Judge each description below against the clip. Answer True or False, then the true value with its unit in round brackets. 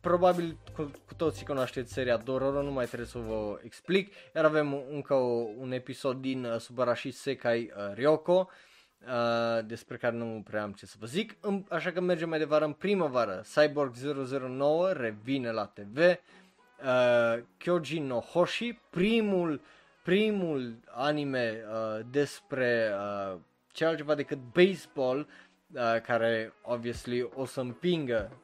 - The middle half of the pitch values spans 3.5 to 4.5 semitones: False (5.1 semitones)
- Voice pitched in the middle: False (130 Hz)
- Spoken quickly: False (140 wpm)